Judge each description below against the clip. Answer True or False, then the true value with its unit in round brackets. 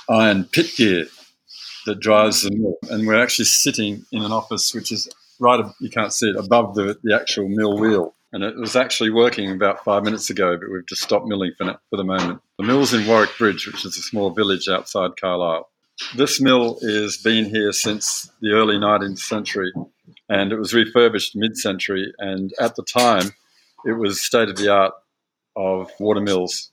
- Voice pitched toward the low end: True (105 Hz)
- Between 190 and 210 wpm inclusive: True (195 wpm)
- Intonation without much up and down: True (2.1 semitones)